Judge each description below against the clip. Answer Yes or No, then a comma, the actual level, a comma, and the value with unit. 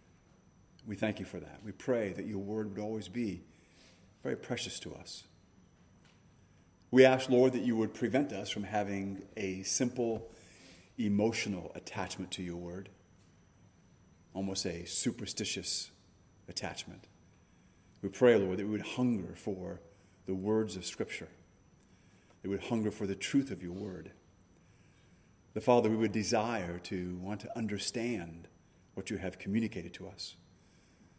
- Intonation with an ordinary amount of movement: Yes, average, 3.0 semitones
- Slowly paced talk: No, average, 145 wpm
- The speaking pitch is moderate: No, very low, 95 Hz